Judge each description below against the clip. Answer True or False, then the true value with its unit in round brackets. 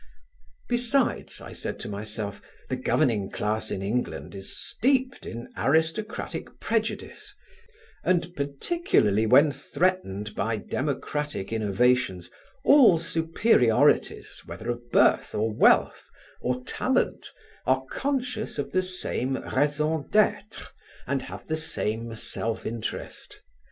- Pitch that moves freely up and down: True (8.6 semitones)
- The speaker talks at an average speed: False (110 wpm)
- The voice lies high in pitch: False (135 Hz)